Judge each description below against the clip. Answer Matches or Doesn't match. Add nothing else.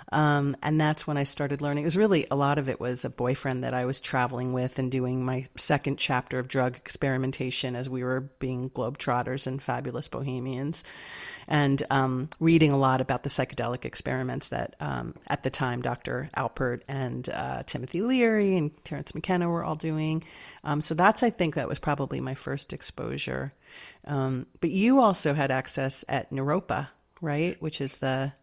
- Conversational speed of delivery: Matches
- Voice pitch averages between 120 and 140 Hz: Matches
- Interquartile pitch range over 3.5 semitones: Doesn't match